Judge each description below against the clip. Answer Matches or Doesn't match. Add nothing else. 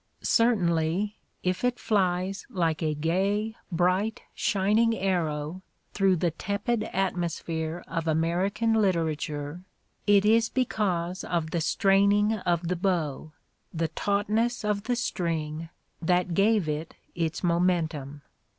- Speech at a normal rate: Doesn't match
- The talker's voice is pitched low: Doesn't match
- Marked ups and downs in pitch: Doesn't match